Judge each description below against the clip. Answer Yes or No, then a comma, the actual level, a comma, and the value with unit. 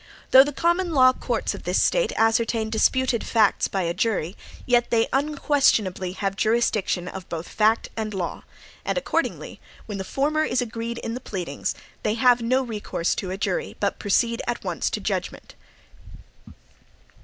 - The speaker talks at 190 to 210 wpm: No, average, 165 wpm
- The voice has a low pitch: No, high, 230 Hz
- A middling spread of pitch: Yes, average, 4.6 semitones